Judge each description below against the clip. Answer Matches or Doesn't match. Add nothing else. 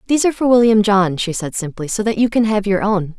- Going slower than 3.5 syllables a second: Doesn't match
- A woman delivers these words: Matches